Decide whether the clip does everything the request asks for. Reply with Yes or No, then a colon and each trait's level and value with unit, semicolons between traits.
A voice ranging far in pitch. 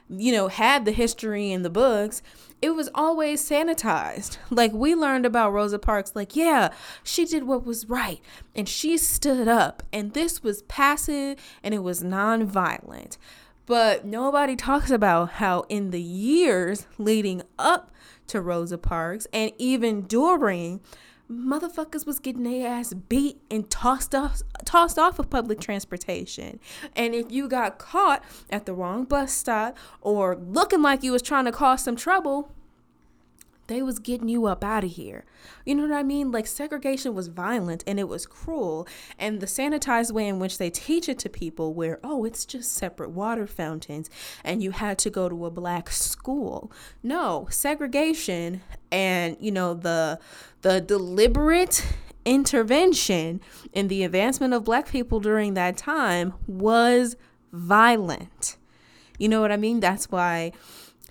Yes: wide, 6.2 semitones